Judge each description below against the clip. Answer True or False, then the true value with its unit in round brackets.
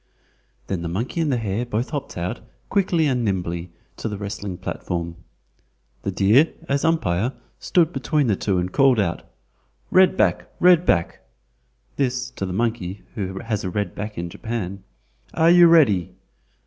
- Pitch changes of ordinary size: False (7.0 semitones)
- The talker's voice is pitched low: True (110 Hz)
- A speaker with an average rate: True (160 wpm)